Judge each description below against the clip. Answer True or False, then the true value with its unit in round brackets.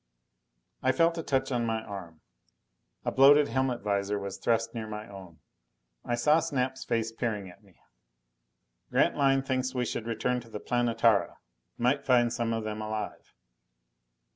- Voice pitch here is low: True (115 Hz)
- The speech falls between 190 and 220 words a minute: False (155 wpm)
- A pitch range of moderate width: True (3.4 semitones)